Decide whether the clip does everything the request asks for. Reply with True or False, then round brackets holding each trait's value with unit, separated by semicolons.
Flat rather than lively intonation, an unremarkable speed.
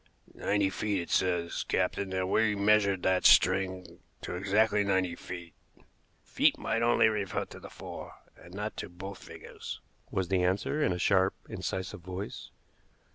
True (2.0 semitones; 155 wpm)